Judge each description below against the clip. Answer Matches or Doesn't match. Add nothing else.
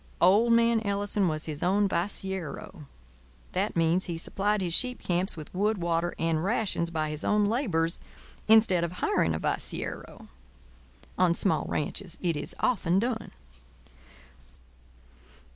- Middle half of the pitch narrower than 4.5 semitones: Matches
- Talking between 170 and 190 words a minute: Doesn't match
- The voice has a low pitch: Doesn't match